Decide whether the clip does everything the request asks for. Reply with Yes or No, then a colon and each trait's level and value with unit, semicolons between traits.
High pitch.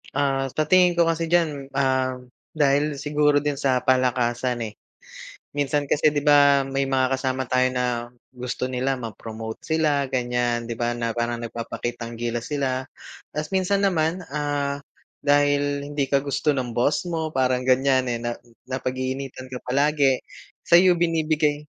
No: low, 135 Hz